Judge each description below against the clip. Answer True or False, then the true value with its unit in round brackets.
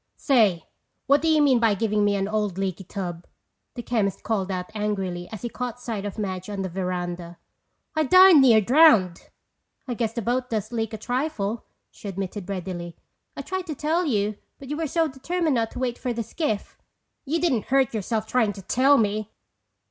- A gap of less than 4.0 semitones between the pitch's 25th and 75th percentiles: False (5.0 semitones)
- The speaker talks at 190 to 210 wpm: True (195 wpm)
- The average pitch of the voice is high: True (220 Hz)